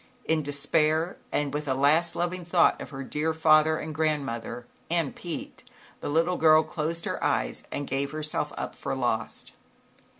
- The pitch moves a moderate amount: No, narrow, 2.2 semitones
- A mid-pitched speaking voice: Yes, medium, 155 Hz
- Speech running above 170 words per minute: No, average, 165 wpm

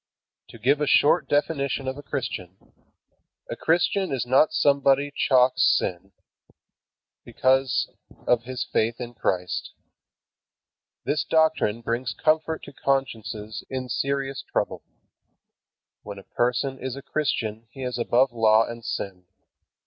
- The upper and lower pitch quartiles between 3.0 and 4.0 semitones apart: Yes, average, 3.3 semitones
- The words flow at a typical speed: No, slow, 130 wpm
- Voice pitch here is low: Yes, low, 130 Hz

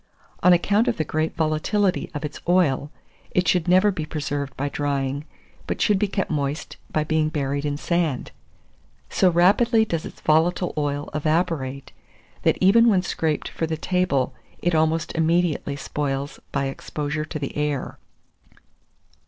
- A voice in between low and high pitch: Yes, medium, 155 Hz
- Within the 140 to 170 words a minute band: Yes, average, 155 wpm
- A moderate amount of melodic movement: Yes, average, 3.7 semitones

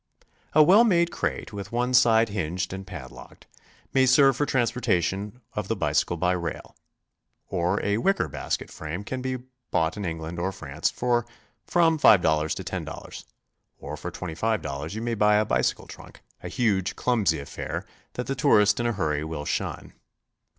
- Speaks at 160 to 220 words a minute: Yes, average, 165 wpm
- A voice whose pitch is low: Yes, low, 105 Hz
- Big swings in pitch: Yes, wide, 6.2 semitones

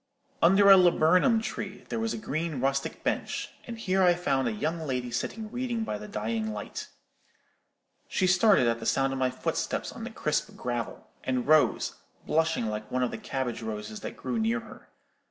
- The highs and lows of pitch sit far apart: Yes, wide, 8.2 semitones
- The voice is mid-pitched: Yes, medium, 150 Hz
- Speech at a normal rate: Yes, average, 190 wpm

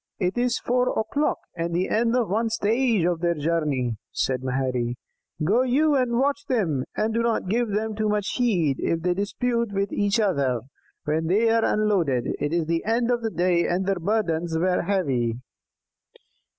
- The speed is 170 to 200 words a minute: Yes, average, 175 wpm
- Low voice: No, high, 195 Hz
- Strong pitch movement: Yes, wide, 5.8 semitones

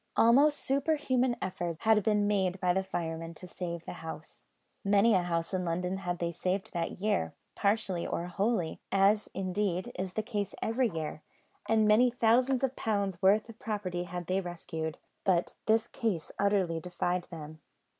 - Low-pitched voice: No, high, 190 Hz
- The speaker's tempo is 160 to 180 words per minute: Yes, average, 165 wpm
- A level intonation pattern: No, average, 3.8 semitones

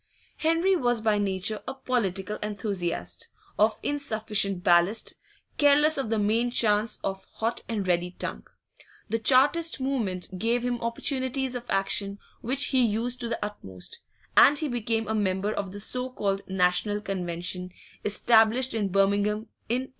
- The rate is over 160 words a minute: No, average, 150 wpm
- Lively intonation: No, average, 3.9 semitones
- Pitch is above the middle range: Yes, high, 215 Hz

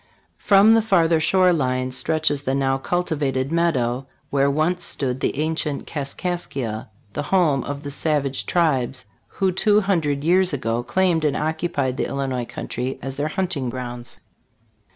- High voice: No, medium, 145 Hz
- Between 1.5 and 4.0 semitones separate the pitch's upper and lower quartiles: No, average, 4.4 semitones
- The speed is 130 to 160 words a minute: Yes, average, 155 wpm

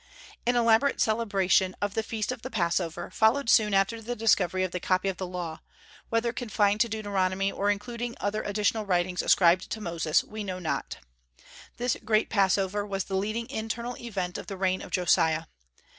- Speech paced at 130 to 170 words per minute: No, average, 180 wpm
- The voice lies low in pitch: No, high, 205 Hz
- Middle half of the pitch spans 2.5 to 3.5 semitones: Yes, average, 3.2 semitones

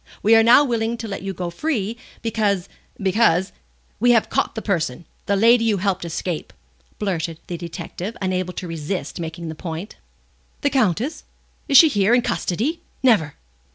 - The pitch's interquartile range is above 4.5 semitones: Yes, average, 4.9 semitones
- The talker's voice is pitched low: No, high, 195 Hz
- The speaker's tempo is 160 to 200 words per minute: Yes, average, 180 wpm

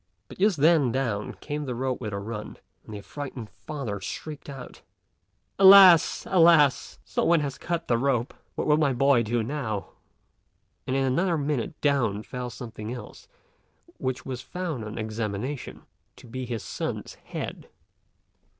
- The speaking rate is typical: Yes, average, 155 wpm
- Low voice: Yes, low, 130 Hz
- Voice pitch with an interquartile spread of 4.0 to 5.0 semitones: Yes, average, 4.5 semitones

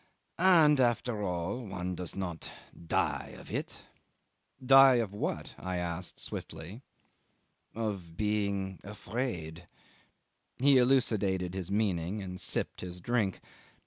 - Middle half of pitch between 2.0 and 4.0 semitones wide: No, average, 4.9 semitones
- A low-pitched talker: Yes, low, 100 Hz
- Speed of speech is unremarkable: No, slow, 115 wpm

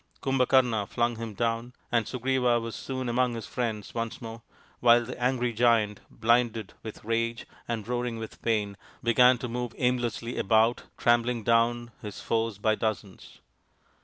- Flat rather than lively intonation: Yes, narrow, 1.4 semitones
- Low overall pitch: Yes, low, 115 Hz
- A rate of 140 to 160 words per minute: Yes, average, 150 wpm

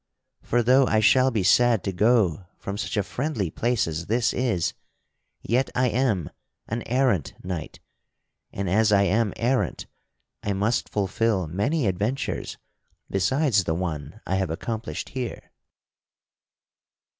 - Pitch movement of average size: Yes, average, 4.5 semitones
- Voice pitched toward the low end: Yes, low, 110 Hz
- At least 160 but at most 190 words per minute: No, slow, 135 wpm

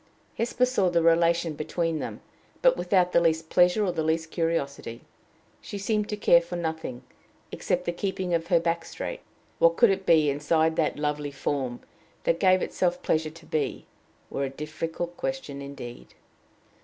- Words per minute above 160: Yes, average, 170 wpm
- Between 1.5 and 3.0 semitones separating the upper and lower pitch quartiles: Yes, average, 2.7 semitones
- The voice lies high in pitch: No, medium, 165 Hz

